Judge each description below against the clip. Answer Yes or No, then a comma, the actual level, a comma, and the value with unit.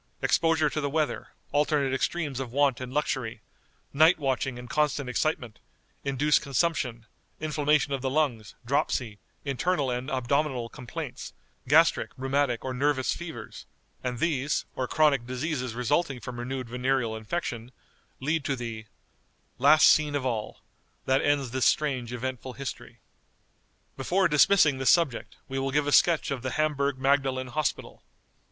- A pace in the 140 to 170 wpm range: Yes, average, 145 wpm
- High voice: No, low, 135 Hz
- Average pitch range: Yes, average, 3.0 semitones